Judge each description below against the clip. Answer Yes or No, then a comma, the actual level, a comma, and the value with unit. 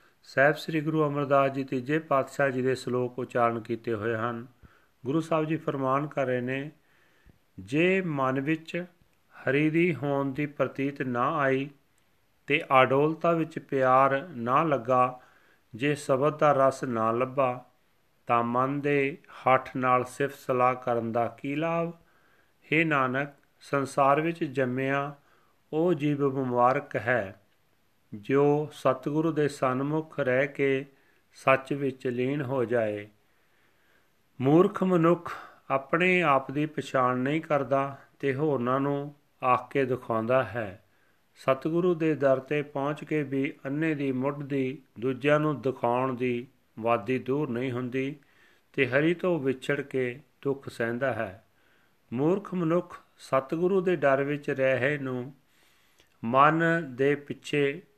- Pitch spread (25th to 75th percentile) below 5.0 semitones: Yes, narrow, 2.6 semitones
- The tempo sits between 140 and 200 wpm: No, average, 130 wpm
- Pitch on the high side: No, low, 135 Hz